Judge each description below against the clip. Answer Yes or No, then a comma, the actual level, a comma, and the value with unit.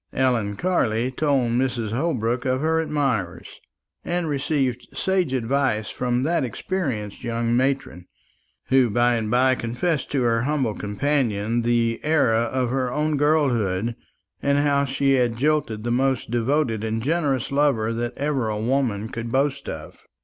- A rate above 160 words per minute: No, average, 150 wpm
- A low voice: Yes, low, 125 Hz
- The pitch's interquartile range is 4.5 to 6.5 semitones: No, average, 3.7 semitones